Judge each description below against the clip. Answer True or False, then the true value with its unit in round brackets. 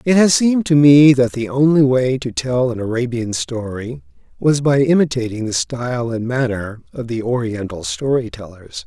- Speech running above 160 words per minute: True (175 wpm)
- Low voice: True (125 Hz)